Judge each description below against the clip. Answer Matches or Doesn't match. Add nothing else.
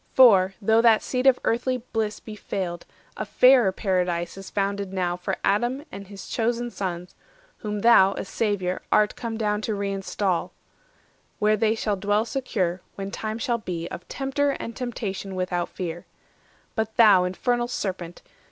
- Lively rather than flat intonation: Doesn't match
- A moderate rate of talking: Matches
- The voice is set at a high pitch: Matches